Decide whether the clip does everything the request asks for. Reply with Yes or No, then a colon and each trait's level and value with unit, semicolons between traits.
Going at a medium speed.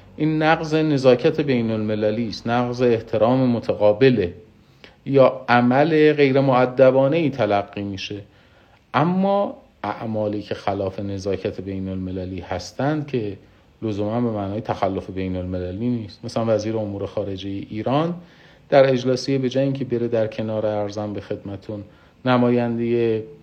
Yes: average, 125 wpm